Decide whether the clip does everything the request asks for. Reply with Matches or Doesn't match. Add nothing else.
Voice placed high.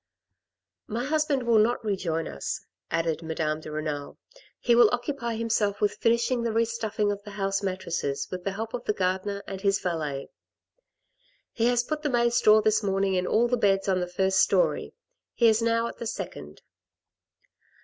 Matches